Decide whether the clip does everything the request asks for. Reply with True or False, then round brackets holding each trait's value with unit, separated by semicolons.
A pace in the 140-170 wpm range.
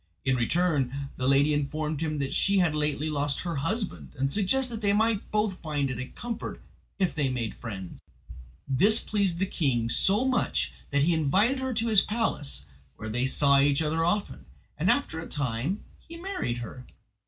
False (185 wpm)